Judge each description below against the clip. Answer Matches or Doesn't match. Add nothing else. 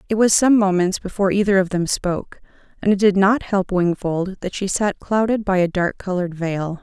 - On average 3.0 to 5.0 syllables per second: Doesn't match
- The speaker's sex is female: Matches